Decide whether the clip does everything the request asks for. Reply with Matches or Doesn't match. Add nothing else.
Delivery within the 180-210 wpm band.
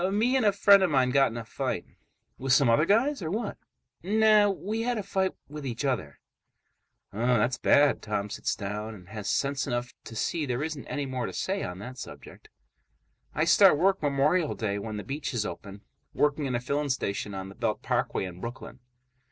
Matches